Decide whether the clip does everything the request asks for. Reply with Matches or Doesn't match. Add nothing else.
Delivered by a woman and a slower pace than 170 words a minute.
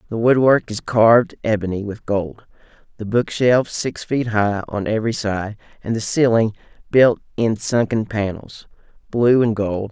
Doesn't match